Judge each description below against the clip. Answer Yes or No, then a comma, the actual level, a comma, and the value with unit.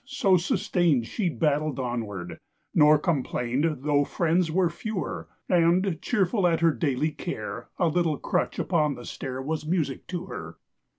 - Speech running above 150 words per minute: No, average, 145 wpm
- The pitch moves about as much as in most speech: Yes, average, 3.9 semitones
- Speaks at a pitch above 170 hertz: No, medium, 160 Hz